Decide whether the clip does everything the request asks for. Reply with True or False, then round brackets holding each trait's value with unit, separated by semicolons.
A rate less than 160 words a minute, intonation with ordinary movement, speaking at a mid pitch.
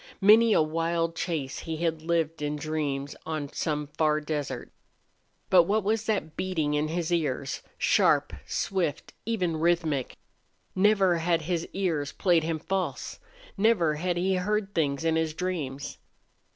True (145 wpm; 3.2 semitones; 165 Hz)